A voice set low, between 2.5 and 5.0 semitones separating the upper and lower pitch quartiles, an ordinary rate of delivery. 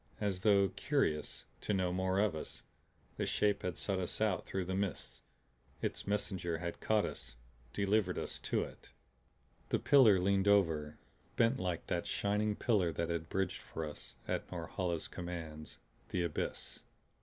Yes: very low, 95 Hz; average, 3.1 semitones; average, 155 wpm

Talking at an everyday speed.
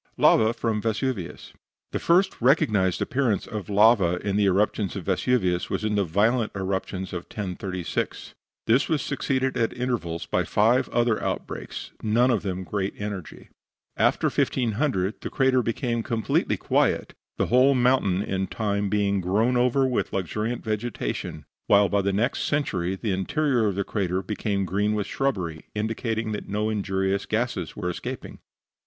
Yes: average, 155 wpm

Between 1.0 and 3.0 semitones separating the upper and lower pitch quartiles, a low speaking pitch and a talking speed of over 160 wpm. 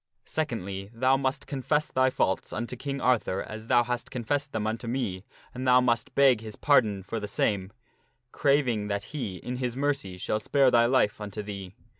No: average, 4.1 semitones; low, 120 Hz; average, 190 wpm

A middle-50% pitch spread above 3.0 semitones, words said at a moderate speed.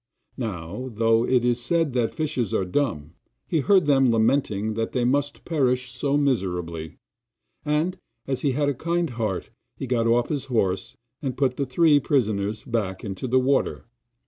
Yes: average, 4.5 semitones; average, 170 wpm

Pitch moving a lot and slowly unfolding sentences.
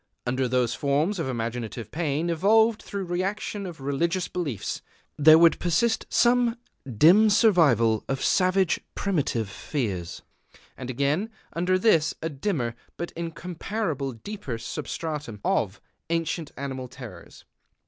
Yes: wide, 6.3 semitones; slow, 120 wpm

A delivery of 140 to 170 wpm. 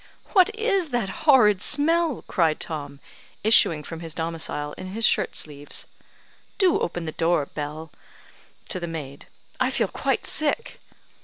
Yes: average, 145 wpm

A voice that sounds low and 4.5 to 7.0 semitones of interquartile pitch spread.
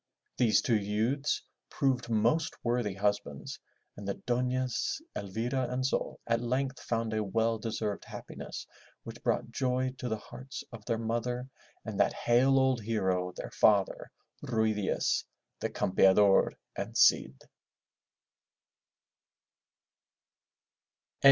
No: low, 115 Hz; average, 3.2 semitones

